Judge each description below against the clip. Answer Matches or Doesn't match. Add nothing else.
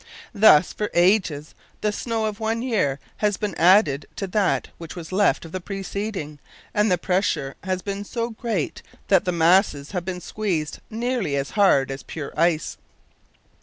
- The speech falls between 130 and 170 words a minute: Matches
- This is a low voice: Doesn't match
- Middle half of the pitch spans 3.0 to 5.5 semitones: Matches